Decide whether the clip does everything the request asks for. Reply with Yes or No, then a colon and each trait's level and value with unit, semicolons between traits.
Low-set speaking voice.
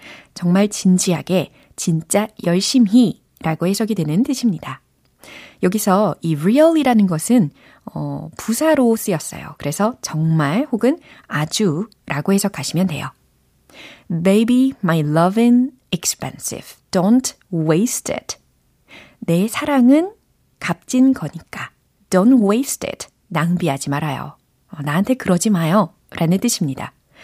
No: high, 195 Hz